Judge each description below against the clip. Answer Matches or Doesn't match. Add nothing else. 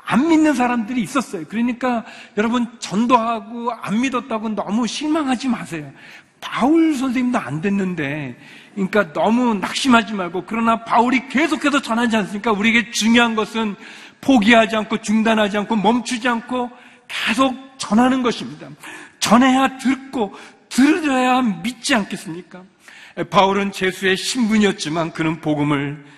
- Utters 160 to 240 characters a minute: Doesn't match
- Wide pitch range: Doesn't match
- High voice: Matches